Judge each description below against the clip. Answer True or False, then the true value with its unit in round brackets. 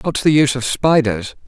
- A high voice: False (135 Hz)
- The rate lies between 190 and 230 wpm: True (205 wpm)